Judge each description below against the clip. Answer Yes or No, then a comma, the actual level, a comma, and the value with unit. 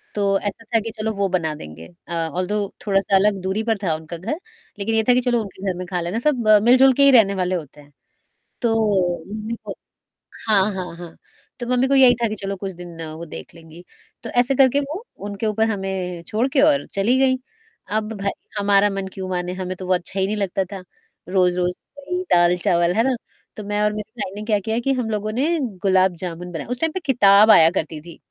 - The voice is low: No, high, 200 Hz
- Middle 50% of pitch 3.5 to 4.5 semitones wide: Yes, average, 3.9 semitones